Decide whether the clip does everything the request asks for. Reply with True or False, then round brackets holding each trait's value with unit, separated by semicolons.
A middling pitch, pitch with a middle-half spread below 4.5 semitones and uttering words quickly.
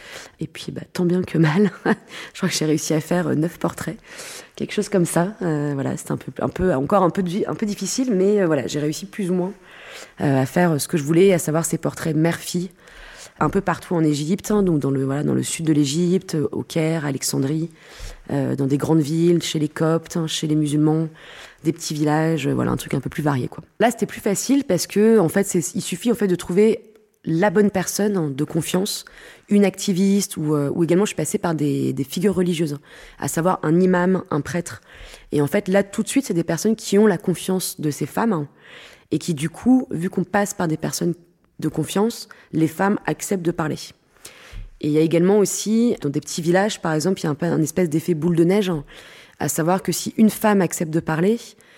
True (175 Hz; 4.1 semitones; 230 wpm)